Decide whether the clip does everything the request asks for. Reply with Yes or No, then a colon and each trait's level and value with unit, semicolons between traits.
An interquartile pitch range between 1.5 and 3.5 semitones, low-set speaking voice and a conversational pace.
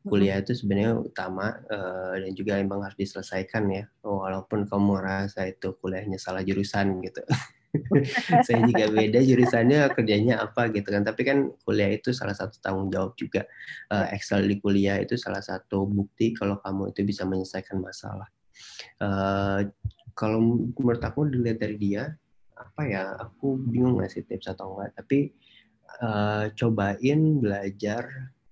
No: average, 3.0 semitones; low, 100 Hz; fast, 145 wpm